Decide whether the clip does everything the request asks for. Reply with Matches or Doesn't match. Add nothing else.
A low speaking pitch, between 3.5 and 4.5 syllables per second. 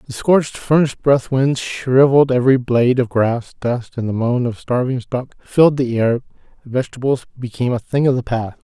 Doesn't match